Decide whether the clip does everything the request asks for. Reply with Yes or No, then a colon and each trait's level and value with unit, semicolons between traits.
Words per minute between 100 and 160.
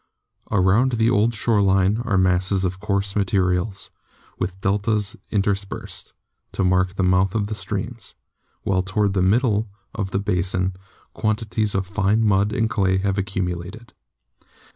Yes: average, 140 wpm